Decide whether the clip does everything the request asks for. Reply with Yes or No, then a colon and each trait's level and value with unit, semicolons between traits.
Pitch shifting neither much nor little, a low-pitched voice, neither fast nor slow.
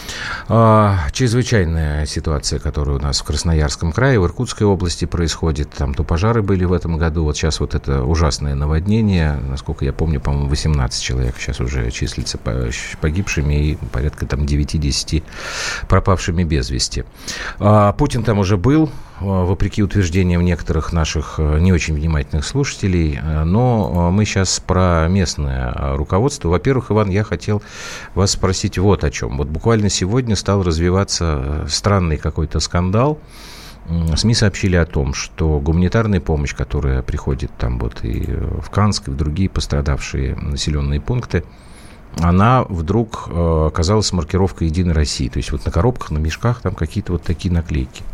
Yes: average, 4.9 semitones; very low, 85 Hz; average, 140 wpm